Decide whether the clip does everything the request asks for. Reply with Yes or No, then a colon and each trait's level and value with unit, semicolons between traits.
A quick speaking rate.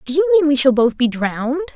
Yes: fast, 275 wpm